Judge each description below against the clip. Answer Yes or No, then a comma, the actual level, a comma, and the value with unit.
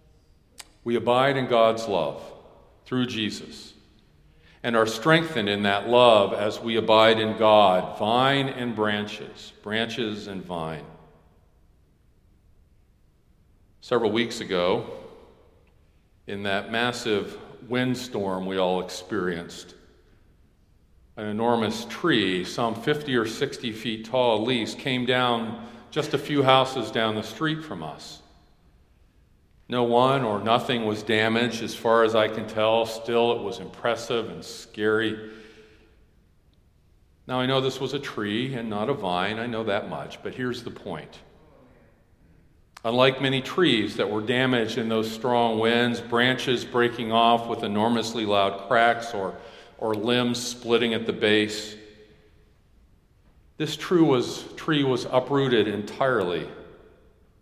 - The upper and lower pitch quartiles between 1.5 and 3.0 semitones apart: No, average, 3.7 semitones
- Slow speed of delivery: Yes, slow, 130 wpm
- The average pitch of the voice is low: Yes, low, 110 Hz